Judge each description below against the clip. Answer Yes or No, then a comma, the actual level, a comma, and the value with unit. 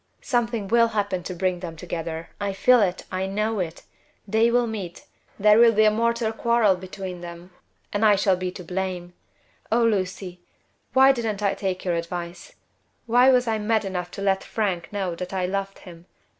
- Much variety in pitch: No, average, 3.7 semitones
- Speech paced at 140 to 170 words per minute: No, average, 185 wpm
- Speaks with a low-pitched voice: No, high, 195 Hz